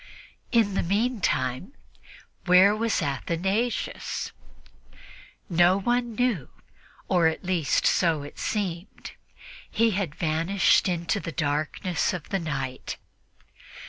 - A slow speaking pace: Yes, slow, 105 wpm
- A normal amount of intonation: Yes, average, 4.1 semitones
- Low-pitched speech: No, medium, 180 Hz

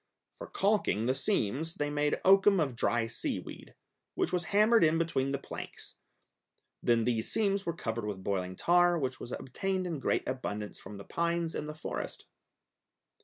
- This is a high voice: No, medium, 150 Hz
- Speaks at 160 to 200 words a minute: Yes, average, 170 wpm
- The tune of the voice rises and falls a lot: Yes, wide, 7.0 semitones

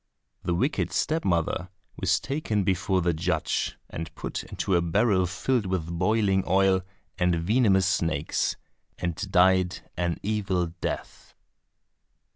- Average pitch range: No, narrow, 2.2 semitones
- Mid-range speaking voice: No, very low, 95 Hz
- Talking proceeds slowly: Yes, slow, 125 wpm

